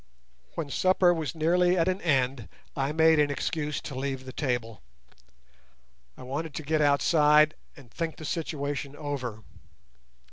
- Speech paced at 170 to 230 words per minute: No, average, 145 wpm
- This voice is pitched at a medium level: Yes, medium, 150 Hz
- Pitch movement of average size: Yes, average, 3.0 semitones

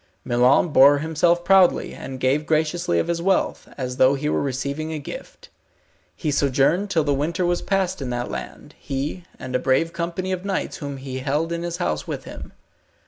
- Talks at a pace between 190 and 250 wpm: Yes, average, 195 wpm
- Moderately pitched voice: Yes, medium, 150 Hz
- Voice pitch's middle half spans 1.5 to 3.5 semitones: No, average, 4.5 semitones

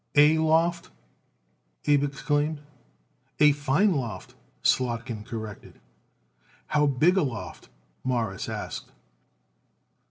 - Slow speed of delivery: Yes, slow, 90 wpm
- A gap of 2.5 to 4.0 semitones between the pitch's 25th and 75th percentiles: No, average, 4.8 semitones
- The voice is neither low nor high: Yes, medium, 145 Hz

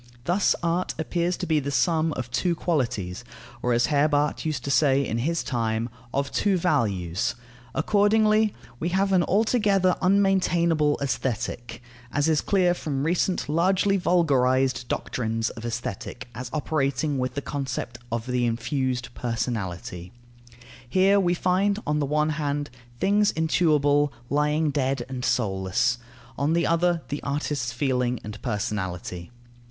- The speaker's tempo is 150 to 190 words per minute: No, average, 140 wpm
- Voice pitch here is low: No, medium, 145 Hz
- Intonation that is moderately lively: No, wide, 5.9 semitones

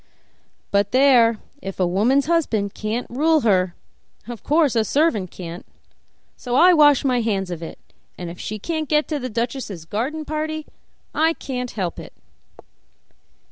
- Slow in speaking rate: No, average, 155 wpm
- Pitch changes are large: Yes, wide, 7.0 semitones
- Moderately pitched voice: No, high, 245 Hz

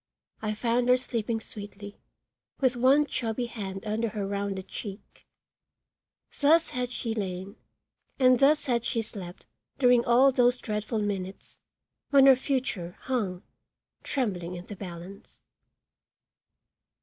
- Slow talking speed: Yes, slow, 125 wpm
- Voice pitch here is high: Yes, high, 225 Hz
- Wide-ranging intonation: No, average, 4.1 semitones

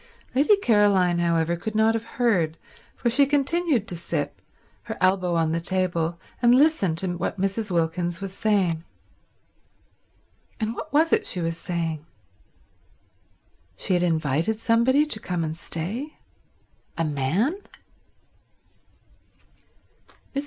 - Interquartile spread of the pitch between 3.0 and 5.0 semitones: No, wide, 5.5 semitones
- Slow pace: Yes, slow, 125 wpm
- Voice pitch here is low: No, medium, 185 Hz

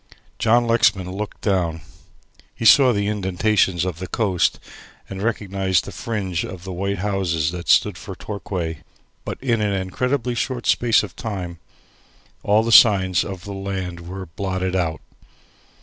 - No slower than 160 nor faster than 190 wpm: No, average, 145 wpm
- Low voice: Yes, very low, 95 Hz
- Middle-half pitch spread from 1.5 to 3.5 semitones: Yes, average, 2.9 semitones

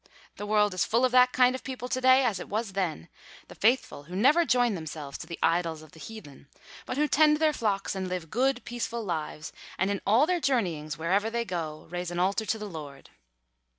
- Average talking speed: No, fast, 220 wpm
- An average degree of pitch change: No, wide, 6.8 semitones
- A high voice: Yes, high, 205 Hz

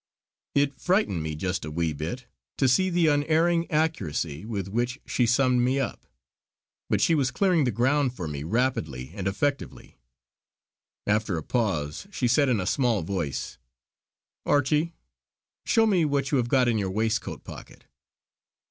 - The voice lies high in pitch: No, low, 125 Hz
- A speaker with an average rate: Yes, average, 155 wpm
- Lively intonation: Yes, wide, 7.0 semitones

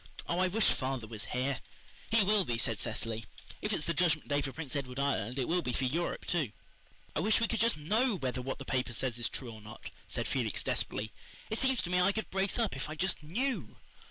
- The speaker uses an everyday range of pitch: No, wide, 7.2 semitones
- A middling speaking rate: No, fast, 240 wpm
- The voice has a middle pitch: Yes, medium, 150 Hz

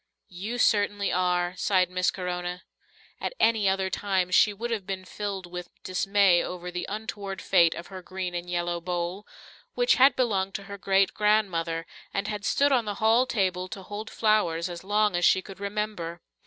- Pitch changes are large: No, average, 2.8 semitones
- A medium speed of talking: Yes, average, 180 wpm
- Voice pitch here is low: No, high, 190 Hz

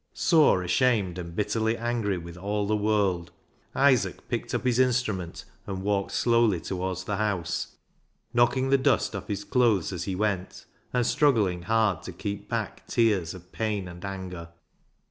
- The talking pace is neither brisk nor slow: Yes, average, 160 wpm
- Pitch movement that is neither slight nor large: Yes, average, 4.2 semitones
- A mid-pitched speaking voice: No, low, 100 Hz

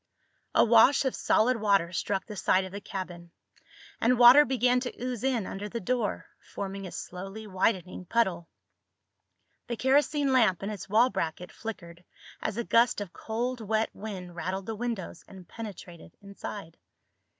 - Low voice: No, high, 210 Hz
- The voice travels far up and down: No, average, 4.1 semitones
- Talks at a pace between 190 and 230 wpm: No, average, 160 wpm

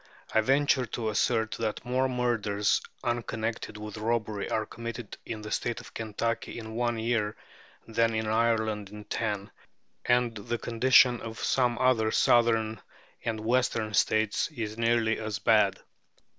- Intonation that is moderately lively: No, narrow, 1.6 semitones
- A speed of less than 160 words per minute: Yes, average, 145 wpm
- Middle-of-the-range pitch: No, low, 115 Hz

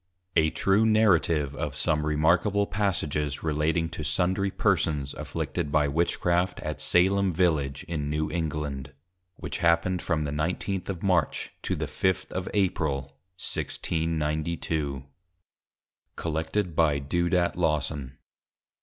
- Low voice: Yes, very low, 80 Hz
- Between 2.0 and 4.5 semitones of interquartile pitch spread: Yes, average, 3.2 semitones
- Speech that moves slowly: Yes, slow, 120 wpm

